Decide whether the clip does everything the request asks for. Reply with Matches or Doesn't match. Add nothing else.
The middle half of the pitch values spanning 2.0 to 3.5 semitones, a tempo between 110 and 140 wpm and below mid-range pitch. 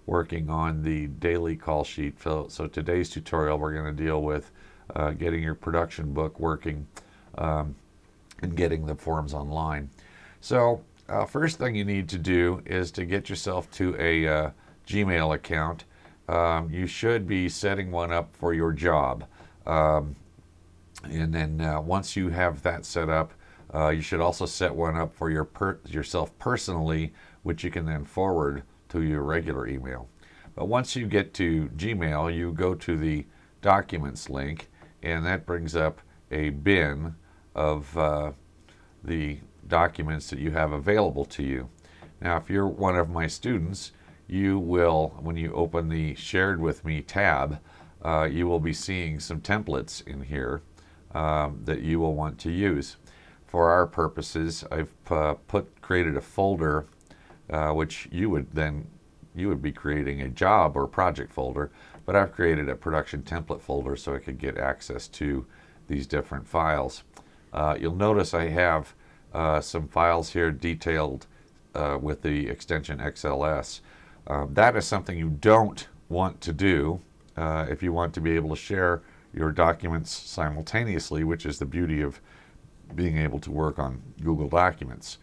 Doesn't match